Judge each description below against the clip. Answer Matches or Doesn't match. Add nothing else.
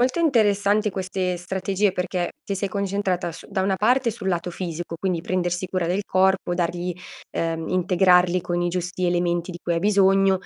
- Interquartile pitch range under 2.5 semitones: Matches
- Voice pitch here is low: Doesn't match